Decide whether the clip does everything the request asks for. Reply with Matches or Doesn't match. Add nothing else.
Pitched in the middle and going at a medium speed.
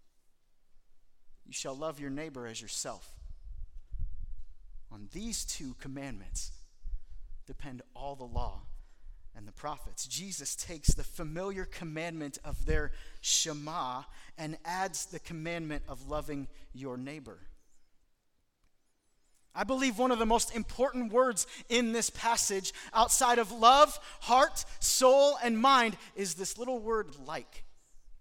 Doesn't match